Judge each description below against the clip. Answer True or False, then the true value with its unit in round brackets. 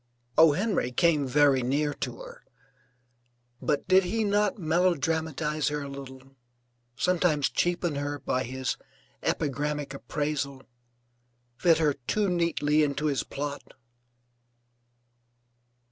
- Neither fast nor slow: False (110 wpm)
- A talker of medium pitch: True (150 Hz)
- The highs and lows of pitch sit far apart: False (3.6 semitones)